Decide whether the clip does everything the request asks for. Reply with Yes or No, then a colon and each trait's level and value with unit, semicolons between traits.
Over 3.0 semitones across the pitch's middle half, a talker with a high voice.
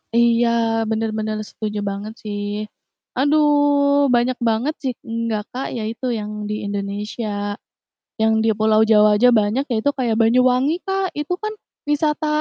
Yes: average, 3.7 semitones; high, 230 Hz